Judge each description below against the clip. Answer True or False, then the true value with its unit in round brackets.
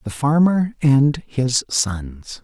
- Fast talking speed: False (125 wpm)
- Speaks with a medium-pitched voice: True (150 Hz)